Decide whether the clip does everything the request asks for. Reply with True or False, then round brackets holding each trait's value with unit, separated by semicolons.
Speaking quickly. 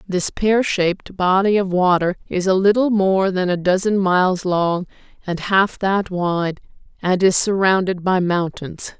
False (160 wpm)